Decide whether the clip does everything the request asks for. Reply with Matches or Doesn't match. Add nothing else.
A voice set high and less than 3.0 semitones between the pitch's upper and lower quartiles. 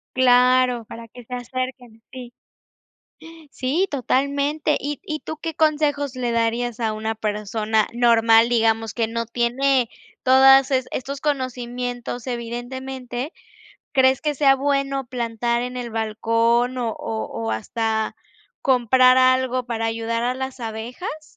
Matches